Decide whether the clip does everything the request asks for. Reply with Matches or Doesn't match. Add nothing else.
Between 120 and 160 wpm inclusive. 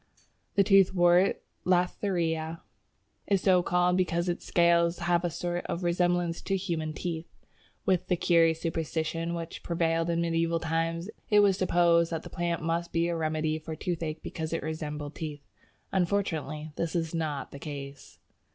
Matches